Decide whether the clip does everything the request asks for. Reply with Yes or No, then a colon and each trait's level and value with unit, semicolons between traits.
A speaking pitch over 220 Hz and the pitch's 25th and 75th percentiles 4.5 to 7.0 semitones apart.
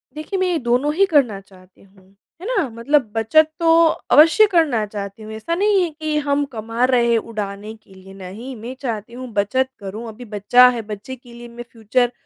Yes: high, 235 Hz; wide, 5.6 semitones